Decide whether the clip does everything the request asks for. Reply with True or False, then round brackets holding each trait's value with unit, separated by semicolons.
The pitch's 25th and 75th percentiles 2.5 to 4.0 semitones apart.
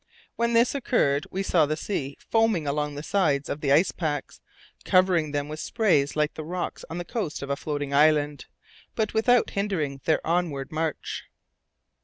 False (5.0 semitones)